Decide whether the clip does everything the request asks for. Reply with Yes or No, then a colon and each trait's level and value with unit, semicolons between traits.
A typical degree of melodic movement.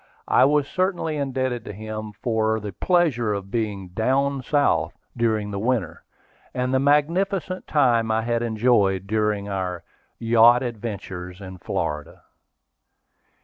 Yes: average, 4.5 semitones